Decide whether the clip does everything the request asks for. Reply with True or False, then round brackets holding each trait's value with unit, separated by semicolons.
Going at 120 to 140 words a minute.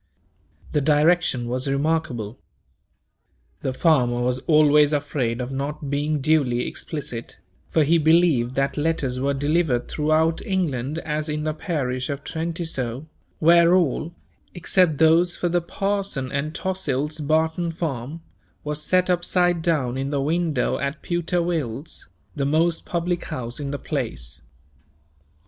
True (135 wpm)